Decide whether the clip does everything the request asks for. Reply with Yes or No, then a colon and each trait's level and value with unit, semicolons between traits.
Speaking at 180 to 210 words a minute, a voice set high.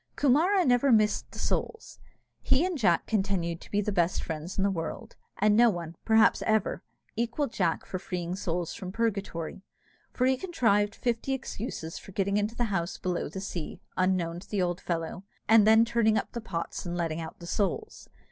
Yes: average, 185 wpm; high, 200 Hz